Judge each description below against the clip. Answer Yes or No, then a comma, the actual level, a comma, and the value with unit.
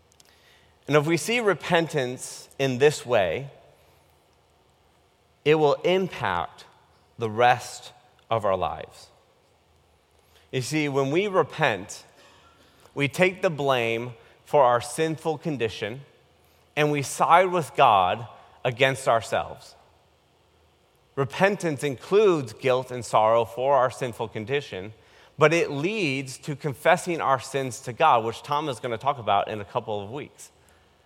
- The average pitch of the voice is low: Yes, low, 130 Hz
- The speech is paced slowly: Yes, slow, 130 wpm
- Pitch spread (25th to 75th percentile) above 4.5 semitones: Yes, average, 5.2 semitones